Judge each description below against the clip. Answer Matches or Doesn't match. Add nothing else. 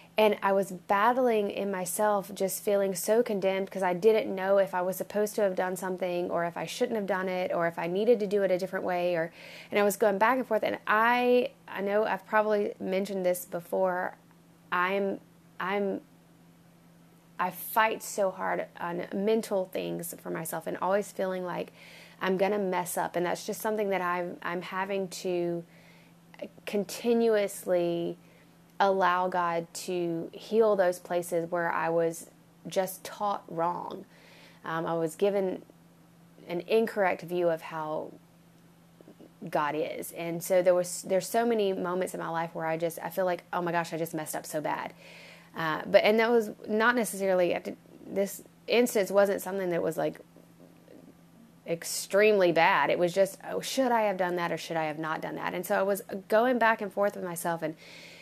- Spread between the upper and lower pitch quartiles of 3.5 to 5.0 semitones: Doesn't match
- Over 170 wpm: Matches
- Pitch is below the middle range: Doesn't match